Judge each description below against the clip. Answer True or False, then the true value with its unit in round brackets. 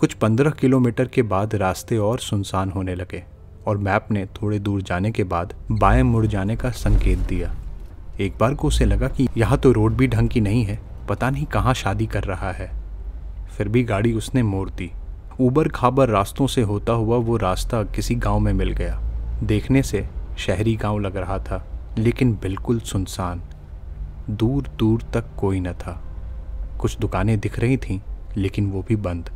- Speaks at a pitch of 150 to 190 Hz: False (105 Hz)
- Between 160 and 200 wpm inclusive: True (180 wpm)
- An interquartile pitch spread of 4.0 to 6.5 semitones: True (4.3 semitones)